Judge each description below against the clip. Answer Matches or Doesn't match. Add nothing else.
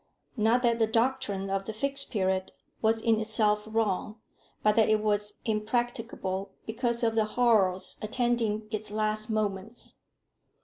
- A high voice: Matches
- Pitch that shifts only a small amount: Matches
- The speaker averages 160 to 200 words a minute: Doesn't match